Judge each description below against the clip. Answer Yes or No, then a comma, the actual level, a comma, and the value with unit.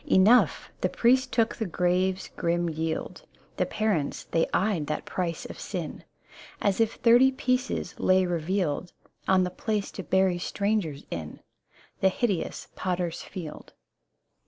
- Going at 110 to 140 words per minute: Yes, slow, 135 wpm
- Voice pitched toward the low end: No, medium, 185 Hz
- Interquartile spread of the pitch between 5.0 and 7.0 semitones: No, average, 4.0 semitones